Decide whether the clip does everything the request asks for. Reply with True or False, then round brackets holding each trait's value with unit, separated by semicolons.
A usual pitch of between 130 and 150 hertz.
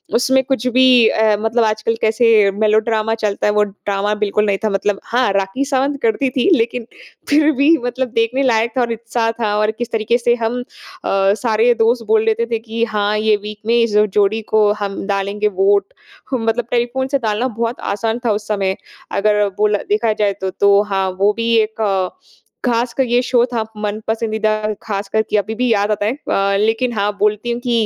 False (220 Hz)